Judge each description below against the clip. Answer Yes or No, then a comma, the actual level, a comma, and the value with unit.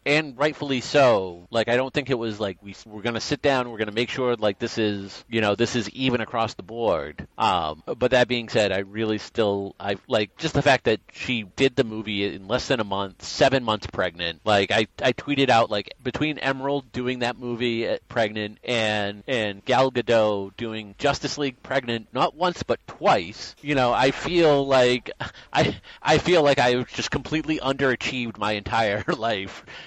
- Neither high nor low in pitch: No, low, 120 Hz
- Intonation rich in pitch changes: No, average, 4.0 semitones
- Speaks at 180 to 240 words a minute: Yes, average, 195 wpm